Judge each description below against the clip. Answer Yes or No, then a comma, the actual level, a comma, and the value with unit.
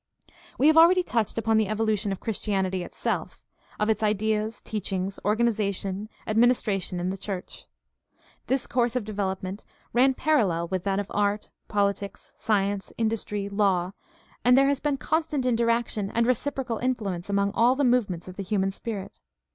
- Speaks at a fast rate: No, average, 160 wpm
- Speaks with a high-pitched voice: Yes, high, 215 Hz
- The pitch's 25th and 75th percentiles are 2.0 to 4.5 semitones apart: Yes, average, 3.3 semitones